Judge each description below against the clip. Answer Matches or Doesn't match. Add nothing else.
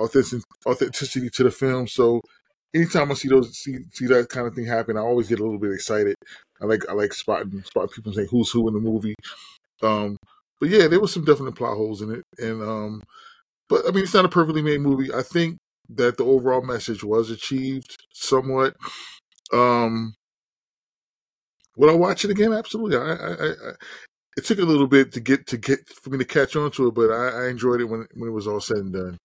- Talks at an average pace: Doesn't match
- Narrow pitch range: Doesn't match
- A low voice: Matches